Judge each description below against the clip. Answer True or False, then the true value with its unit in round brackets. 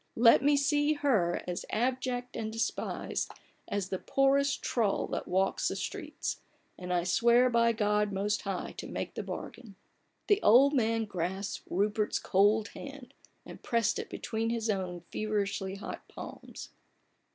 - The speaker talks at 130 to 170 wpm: True (150 wpm)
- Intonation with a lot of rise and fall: False (4.0 semitones)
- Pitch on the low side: False (220 Hz)